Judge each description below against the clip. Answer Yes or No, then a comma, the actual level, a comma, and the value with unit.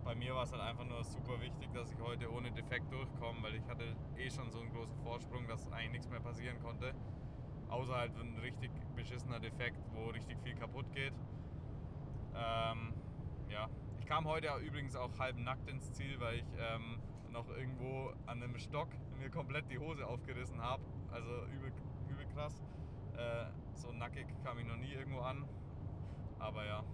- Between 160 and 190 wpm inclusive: Yes, average, 180 wpm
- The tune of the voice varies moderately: No, narrow, 2.0 semitones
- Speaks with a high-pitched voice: No, low, 120 Hz